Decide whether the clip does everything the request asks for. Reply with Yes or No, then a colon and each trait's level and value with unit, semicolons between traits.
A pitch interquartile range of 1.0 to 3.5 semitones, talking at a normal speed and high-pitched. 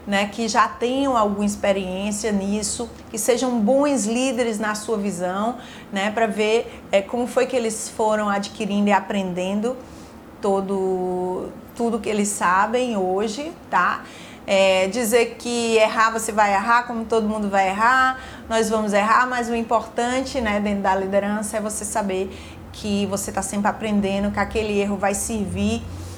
Yes: average, 2.8 semitones; average, 155 wpm; high, 215 Hz